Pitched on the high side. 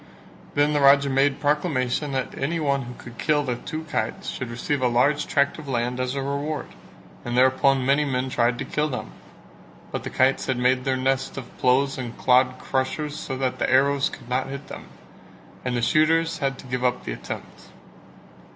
No: low, 135 Hz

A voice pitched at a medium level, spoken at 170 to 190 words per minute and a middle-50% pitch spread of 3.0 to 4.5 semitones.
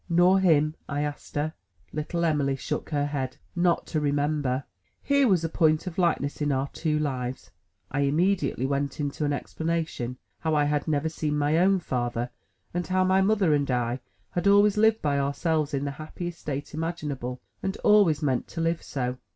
Yes: medium, 150 Hz; average, 185 wpm; average, 3.4 semitones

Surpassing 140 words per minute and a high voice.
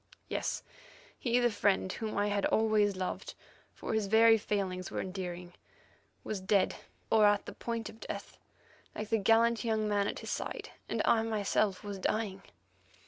Yes: average, 165 wpm; high, 210 Hz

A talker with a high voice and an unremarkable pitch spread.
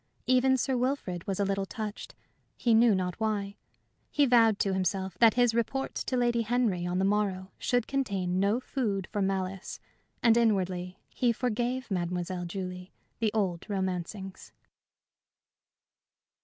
Yes: high, 200 Hz; average, 4.1 semitones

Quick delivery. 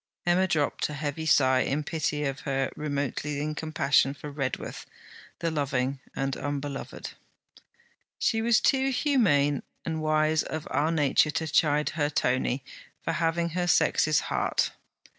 No: average, 140 wpm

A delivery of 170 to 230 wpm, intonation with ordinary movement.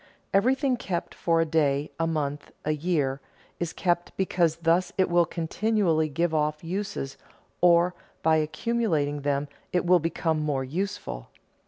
No: average, 145 wpm; average, 3.0 semitones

